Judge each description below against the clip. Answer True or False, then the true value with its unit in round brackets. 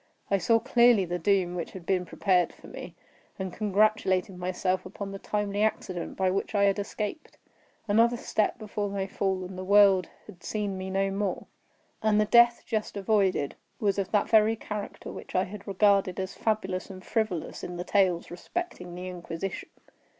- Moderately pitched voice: False (195 Hz)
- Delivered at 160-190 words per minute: True (180 wpm)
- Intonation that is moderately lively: False (2.3 semitones)